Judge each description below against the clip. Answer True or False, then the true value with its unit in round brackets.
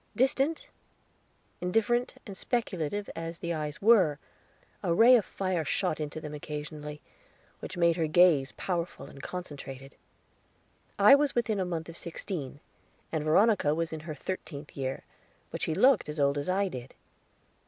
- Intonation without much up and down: False (4.8 semitones)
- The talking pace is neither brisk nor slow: True (155 wpm)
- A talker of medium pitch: True (165 Hz)